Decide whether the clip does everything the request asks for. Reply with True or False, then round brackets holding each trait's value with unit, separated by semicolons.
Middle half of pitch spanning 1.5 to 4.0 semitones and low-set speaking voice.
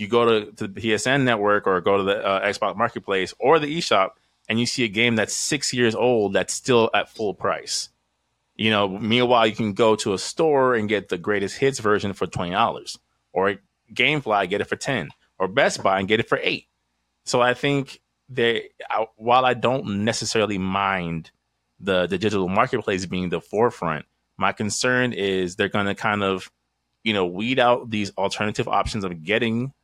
True (3.6 semitones; 105 Hz)